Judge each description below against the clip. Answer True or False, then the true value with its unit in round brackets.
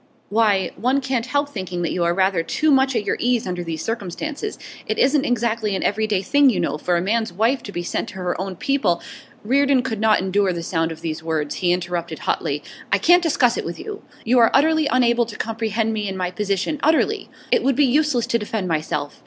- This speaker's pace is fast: True (230 wpm)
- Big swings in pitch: True (6.5 semitones)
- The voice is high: True (215 Hz)